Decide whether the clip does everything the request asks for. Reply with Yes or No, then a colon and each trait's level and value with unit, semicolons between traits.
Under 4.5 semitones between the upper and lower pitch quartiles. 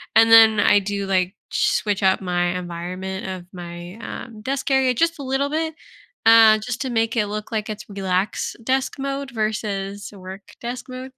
No: average, 4.8 semitones